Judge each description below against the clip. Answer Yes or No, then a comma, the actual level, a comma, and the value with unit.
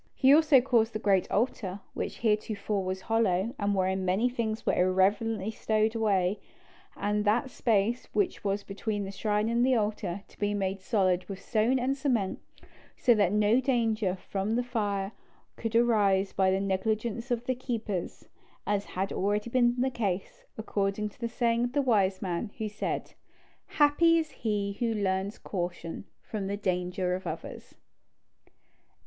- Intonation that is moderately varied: Yes, average, 3.3 semitones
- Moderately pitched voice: No, high, 210 Hz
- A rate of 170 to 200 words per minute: No, average, 160 wpm